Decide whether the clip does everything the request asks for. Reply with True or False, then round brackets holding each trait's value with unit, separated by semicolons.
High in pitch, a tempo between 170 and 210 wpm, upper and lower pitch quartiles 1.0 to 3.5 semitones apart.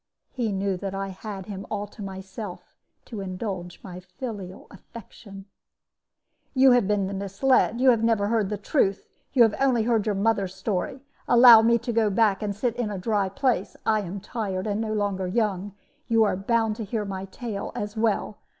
True (205 Hz; 190 wpm; 2.8 semitones)